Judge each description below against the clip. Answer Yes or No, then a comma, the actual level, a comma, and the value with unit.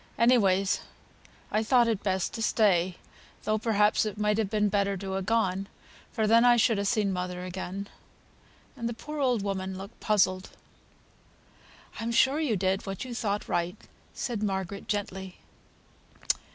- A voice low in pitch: No, high, 205 Hz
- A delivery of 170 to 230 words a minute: No, average, 155 wpm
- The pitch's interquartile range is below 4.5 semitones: Yes, average, 3.0 semitones